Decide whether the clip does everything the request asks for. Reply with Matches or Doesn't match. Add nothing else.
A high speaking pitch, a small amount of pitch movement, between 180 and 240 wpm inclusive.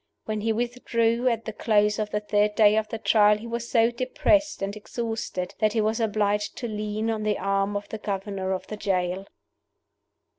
Matches